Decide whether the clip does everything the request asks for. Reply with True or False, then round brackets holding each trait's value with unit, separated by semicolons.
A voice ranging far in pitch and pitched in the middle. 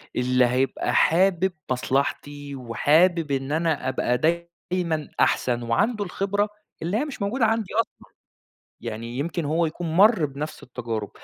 True (6.0 semitones; 155 Hz)